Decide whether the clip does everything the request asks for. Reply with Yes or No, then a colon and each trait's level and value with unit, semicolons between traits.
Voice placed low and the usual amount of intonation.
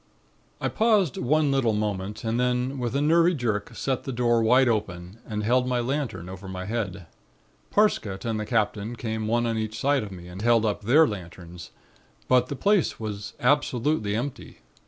Yes: low, 115 Hz; average, 3.7 semitones